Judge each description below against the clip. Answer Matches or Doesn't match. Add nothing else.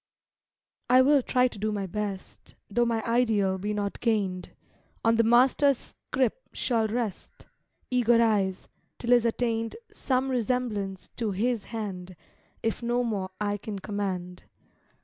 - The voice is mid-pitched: Doesn't match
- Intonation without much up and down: Doesn't match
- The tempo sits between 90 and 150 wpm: Matches